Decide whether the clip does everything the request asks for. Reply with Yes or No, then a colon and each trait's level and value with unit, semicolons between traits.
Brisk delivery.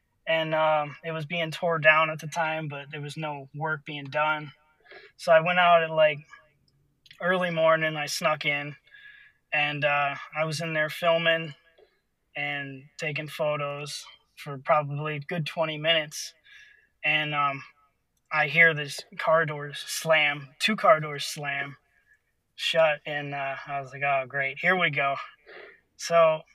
No: average, 155 wpm